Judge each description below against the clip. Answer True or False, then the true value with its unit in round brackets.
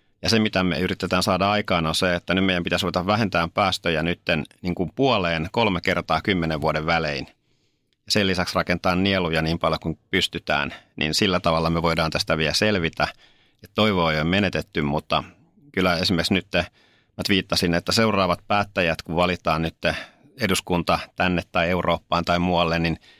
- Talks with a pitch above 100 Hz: False (90 Hz)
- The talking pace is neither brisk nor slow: False (165 wpm)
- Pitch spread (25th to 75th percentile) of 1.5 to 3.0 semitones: True (2.4 semitones)